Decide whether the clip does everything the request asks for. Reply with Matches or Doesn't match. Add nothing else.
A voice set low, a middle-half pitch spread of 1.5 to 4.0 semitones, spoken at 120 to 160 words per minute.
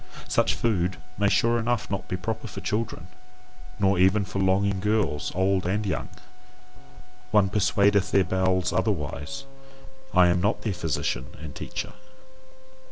Matches